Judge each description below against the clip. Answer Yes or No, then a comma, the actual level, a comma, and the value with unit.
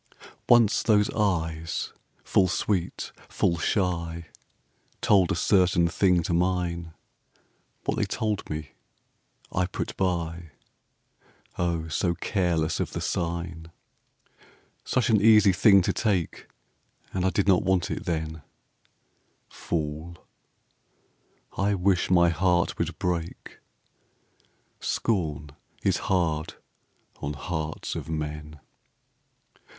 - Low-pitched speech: Yes, very low, 85 Hz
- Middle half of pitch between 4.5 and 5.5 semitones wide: No, average, 2.7 semitones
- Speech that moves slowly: Yes, slow, 105 wpm